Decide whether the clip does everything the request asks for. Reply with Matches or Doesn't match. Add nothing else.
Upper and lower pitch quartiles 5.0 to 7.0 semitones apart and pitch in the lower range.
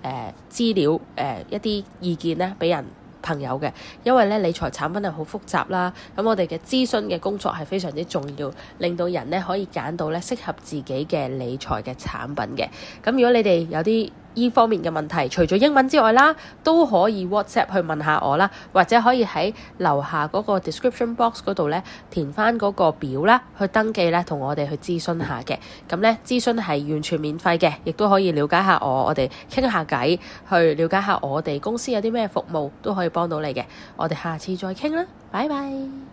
Doesn't match